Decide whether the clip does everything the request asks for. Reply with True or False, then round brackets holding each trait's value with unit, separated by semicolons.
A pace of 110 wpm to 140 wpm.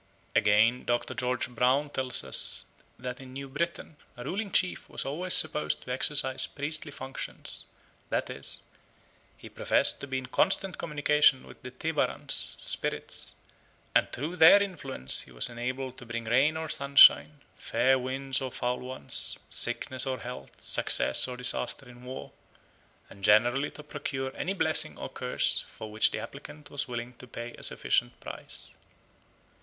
False (155 wpm)